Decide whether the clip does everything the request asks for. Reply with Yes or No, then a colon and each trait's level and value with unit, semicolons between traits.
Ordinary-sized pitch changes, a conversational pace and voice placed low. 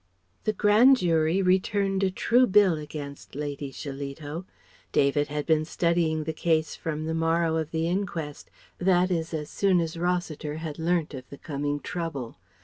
No: average, 3.2 semitones; average, 165 wpm; medium, 160 Hz